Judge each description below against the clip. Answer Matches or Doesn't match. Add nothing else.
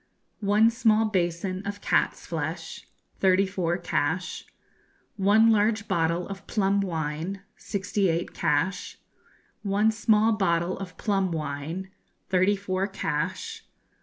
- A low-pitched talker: Doesn't match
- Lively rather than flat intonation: Doesn't match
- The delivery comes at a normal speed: Doesn't match